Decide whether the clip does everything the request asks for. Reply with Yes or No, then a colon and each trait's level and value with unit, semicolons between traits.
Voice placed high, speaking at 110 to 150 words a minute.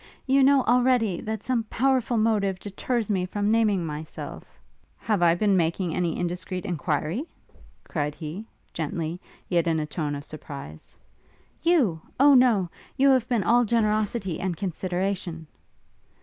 Yes: high, 195 Hz; average, 145 wpm